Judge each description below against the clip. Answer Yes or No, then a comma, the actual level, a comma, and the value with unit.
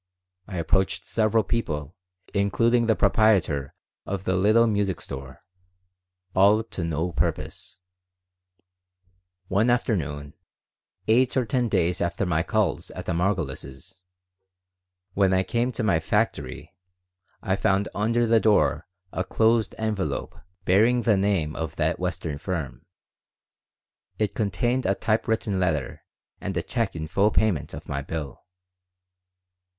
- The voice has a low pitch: Yes, low, 100 Hz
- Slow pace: Yes, slow, 125 wpm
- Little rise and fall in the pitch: No, average, 5.0 semitones